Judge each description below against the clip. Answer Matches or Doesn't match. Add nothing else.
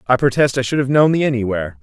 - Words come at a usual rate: Doesn't match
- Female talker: Doesn't match